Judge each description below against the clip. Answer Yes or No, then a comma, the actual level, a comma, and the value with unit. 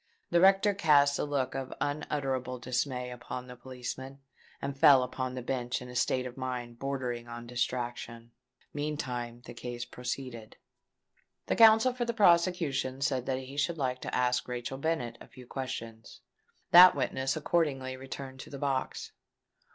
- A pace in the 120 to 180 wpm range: Yes, average, 160 wpm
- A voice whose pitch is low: Yes, low, 130 Hz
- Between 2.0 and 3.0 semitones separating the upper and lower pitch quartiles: Yes, narrow, 2.5 semitones